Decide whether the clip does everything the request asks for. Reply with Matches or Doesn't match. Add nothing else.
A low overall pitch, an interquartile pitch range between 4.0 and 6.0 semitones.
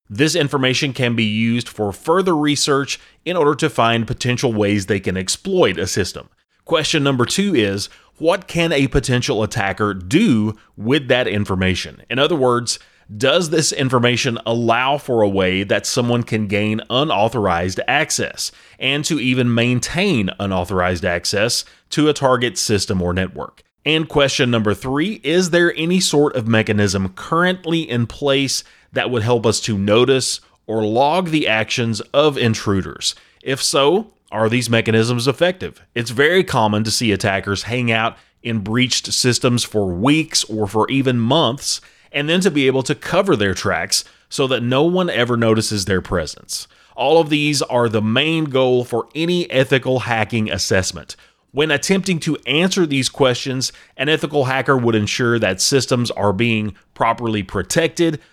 Matches